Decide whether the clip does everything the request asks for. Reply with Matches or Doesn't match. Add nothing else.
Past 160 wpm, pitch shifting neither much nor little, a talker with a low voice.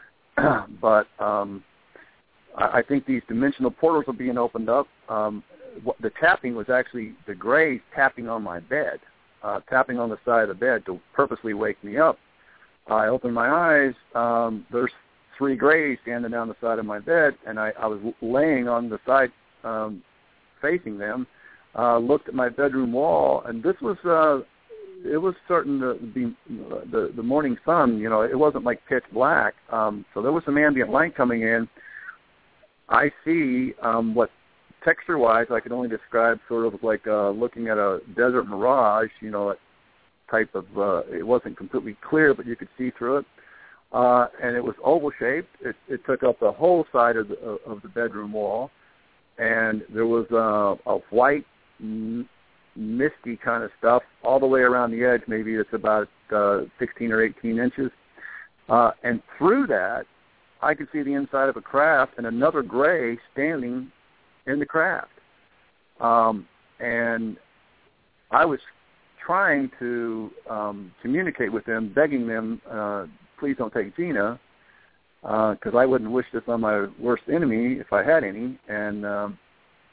Matches